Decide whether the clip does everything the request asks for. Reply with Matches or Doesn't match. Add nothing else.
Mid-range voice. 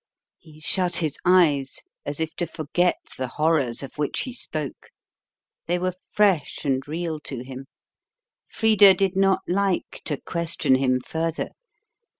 Matches